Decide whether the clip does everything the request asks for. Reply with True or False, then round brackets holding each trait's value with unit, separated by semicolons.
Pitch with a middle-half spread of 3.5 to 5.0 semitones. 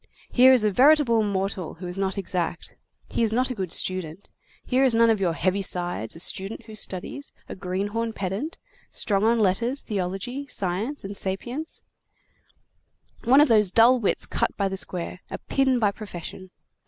True (4.4 semitones)